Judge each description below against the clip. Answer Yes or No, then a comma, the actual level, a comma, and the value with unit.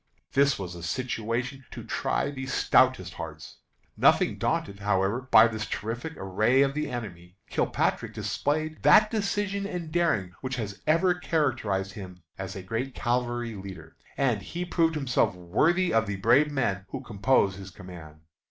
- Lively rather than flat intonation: Yes, wide, 6.9 semitones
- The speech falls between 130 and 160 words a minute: Yes, average, 155 wpm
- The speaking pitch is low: Yes, low, 120 Hz